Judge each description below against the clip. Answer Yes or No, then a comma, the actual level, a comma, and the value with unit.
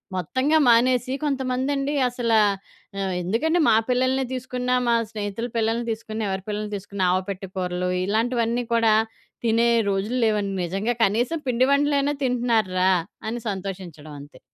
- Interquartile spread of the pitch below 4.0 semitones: No, average, 4.3 semitones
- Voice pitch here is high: Yes, high, 230 Hz